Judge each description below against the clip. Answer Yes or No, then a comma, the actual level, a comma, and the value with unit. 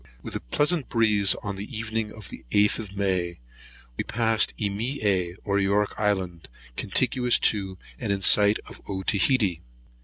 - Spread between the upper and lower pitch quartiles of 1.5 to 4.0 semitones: Yes, narrow, 2.5 semitones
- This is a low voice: Yes, low, 105 Hz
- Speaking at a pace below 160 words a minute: Yes, average, 145 wpm